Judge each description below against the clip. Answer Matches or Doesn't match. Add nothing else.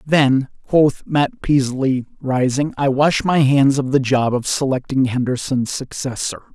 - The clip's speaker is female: Doesn't match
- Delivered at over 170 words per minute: Doesn't match